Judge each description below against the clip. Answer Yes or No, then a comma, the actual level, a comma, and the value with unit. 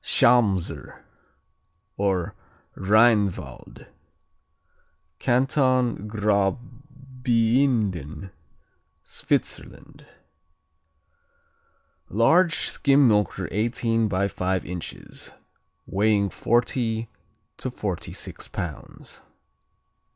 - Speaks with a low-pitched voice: Yes, low, 110 Hz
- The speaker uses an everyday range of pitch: Yes, average, 4.0 semitones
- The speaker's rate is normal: No, slow, 55 wpm